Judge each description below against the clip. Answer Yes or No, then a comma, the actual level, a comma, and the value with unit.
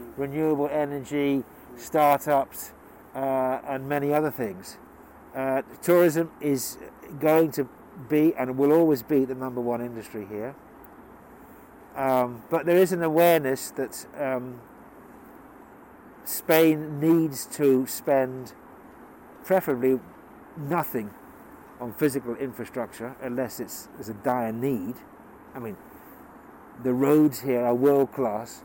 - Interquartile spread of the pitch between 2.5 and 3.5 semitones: Yes, average, 3.2 semitones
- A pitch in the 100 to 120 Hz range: No, low, 135 Hz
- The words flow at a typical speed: No, slow, 115 wpm